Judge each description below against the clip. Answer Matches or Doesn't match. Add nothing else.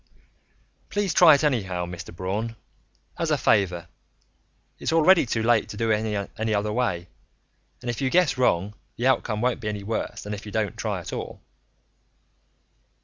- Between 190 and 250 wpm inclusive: Doesn't match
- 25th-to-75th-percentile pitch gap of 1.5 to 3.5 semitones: Doesn't match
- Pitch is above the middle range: Doesn't match